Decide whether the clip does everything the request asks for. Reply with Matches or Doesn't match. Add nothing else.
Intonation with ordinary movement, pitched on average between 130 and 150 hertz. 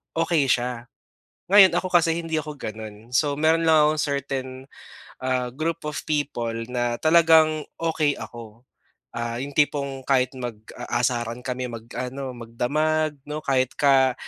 Matches